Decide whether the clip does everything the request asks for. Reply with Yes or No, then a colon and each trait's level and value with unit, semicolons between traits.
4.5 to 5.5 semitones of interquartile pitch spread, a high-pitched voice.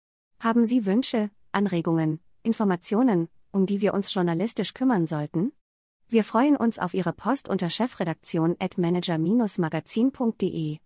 Yes: average, 5.1 semitones; high, 195 Hz